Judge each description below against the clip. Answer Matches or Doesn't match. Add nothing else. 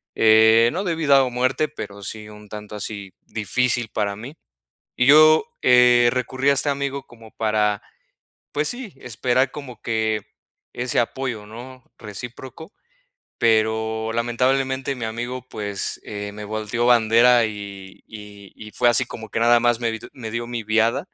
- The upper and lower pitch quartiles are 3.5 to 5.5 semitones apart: Doesn't match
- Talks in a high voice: Doesn't match